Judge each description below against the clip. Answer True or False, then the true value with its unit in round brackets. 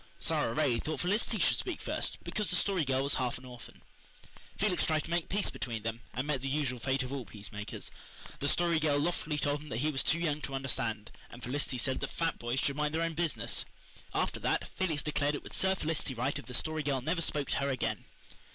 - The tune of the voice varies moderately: True (3.9 semitones)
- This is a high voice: False (145 Hz)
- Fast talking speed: True (235 wpm)